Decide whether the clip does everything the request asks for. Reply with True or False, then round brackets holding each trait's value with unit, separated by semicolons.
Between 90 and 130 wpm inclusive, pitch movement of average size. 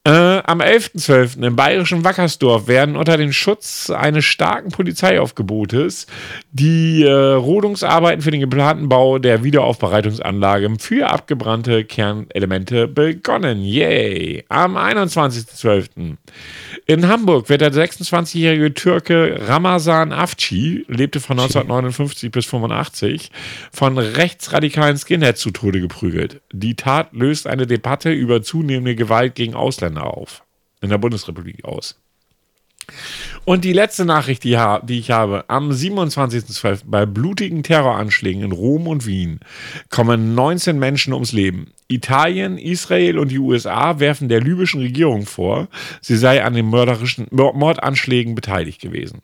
False (125 wpm; 5.7 semitones)